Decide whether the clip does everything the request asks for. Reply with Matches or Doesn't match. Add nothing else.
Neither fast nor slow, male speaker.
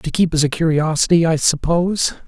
Matches